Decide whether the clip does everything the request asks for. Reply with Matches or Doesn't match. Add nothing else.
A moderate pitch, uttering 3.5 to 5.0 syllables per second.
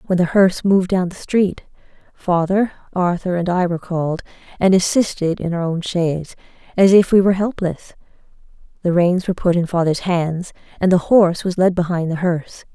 Doesn't match